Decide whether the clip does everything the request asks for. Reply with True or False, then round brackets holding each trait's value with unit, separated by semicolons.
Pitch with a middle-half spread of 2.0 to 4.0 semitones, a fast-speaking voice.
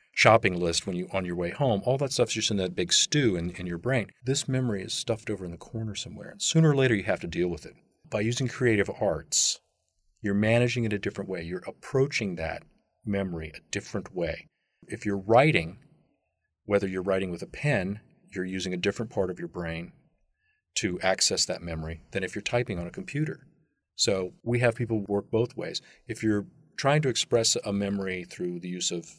False (4.7 semitones; 210 wpm)